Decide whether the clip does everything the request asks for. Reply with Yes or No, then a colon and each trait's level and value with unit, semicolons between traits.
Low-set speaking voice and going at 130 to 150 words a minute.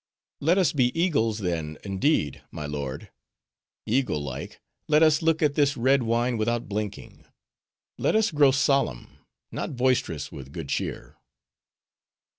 Yes: low, 120 Hz; slow, 135 wpm